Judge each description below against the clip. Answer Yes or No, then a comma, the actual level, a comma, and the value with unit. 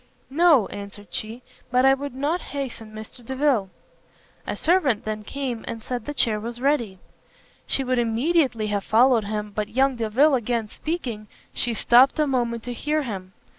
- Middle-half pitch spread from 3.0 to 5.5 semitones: Yes, average, 4.0 semitones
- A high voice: Yes, high, 240 Hz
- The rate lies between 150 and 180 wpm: Yes, average, 170 wpm